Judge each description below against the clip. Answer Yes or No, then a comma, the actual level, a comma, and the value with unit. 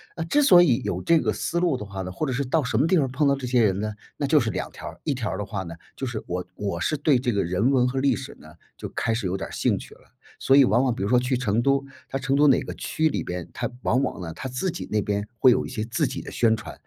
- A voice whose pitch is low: Yes, low, 125 Hz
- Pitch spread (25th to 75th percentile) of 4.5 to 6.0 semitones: Yes, average, 5.1 semitones